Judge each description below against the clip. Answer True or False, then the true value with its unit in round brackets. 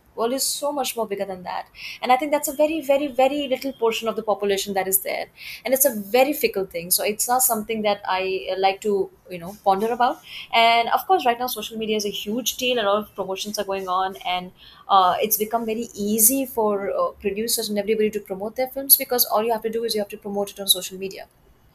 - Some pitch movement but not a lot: True (4.1 semitones)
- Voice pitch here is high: True (215 Hz)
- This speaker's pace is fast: True (250 wpm)